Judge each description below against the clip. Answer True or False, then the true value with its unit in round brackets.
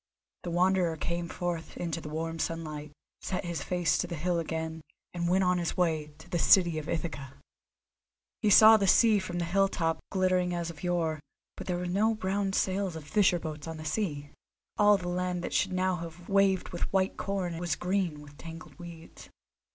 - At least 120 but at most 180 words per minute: False (200 wpm)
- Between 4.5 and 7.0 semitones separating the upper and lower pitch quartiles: False (2.4 semitones)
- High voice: False (175 Hz)